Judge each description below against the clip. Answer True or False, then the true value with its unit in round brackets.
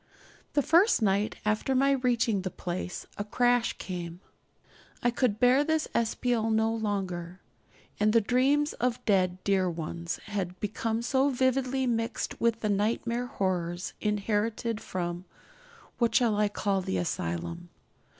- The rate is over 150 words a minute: False (140 wpm)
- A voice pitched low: False (215 Hz)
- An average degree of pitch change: True (4.7 semitones)